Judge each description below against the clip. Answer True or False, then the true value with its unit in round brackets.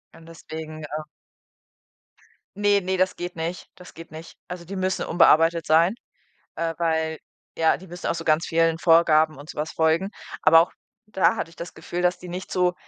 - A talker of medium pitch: True (165 Hz)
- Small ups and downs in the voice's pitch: True (2.0 semitones)